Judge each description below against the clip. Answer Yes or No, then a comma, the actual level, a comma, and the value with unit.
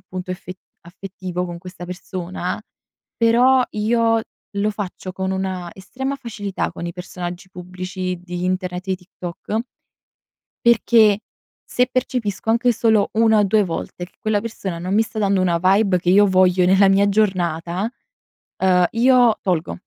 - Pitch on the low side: No, high, 190 Hz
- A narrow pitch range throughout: No, average, 3.1 semitones